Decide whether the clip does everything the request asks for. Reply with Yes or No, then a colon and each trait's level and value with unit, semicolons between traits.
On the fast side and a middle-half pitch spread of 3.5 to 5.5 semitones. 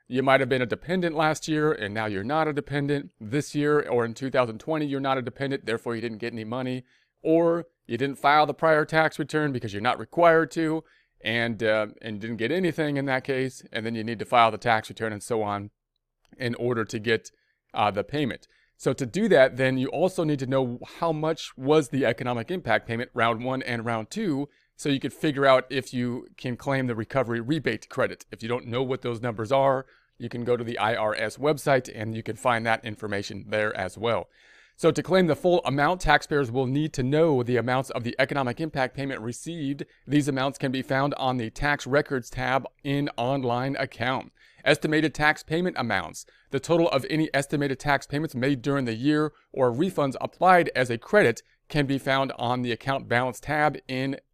Yes: fast, 210 wpm; average, 3.8 semitones